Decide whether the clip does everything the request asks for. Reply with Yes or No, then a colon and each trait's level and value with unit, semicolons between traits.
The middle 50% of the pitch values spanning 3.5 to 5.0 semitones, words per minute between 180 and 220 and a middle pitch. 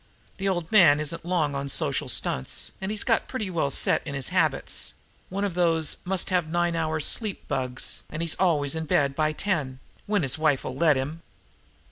Yes: average, 4.2 semitones; average, 190 wpm; medium, 160 Hz